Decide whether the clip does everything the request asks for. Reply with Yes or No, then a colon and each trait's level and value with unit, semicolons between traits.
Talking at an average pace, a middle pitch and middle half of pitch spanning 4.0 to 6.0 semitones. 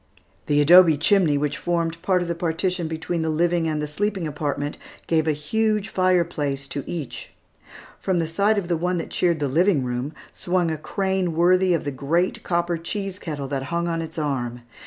No: average, 195 wpm; medium, 165 Hz; average, 3.3 semitones